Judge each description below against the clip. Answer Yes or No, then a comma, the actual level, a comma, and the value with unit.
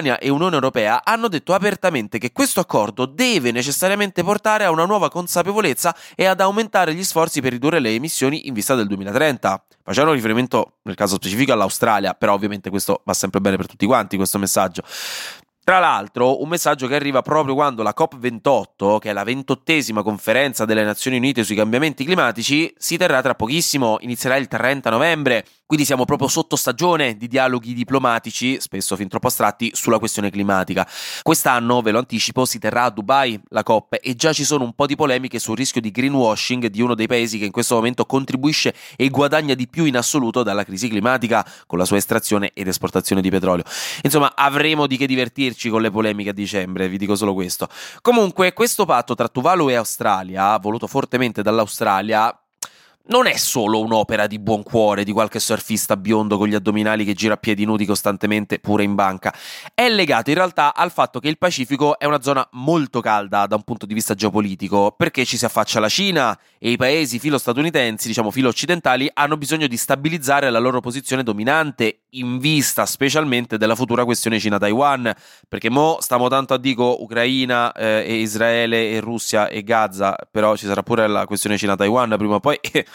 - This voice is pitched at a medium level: No, low, 120 Hz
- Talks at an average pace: No, fast, 185 wpm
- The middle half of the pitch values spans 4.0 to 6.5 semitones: Yes, average, 4.8 semitones